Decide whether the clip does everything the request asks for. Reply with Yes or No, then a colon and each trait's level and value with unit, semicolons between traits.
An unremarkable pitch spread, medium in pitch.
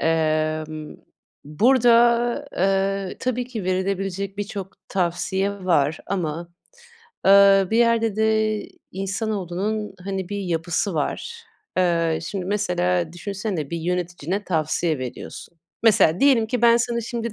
No: average, 4.1 semitones; high, 195 Hz